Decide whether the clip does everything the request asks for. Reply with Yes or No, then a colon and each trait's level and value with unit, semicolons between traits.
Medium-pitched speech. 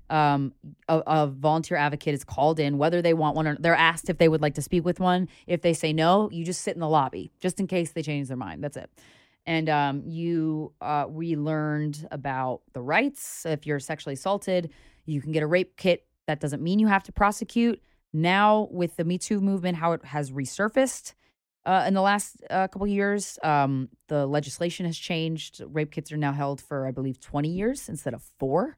Yes: medium, 160 Hz